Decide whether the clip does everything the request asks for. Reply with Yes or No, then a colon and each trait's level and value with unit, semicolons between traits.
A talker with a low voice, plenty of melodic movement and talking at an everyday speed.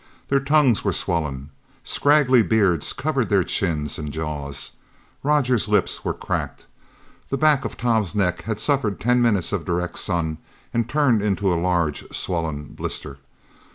Yes: low, 100 Hz; wide, 7.2 semitones; average, 150 wpm